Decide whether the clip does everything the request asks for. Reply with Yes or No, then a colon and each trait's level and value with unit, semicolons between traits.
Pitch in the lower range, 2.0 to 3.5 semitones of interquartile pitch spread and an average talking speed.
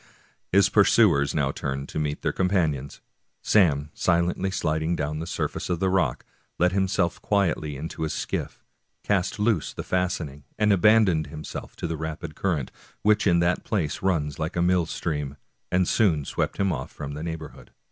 No: very low, 85 Hz; average, 3.9 semitones; average, 170 wpm